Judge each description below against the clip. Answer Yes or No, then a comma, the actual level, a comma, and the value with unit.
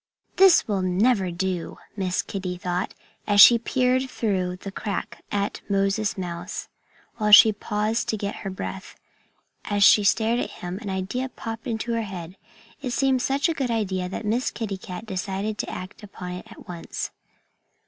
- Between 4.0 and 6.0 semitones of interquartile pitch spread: No, average, 3.5 semitones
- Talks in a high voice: Yes, high, 205 Hz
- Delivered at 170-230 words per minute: Yes, average, 175 wpm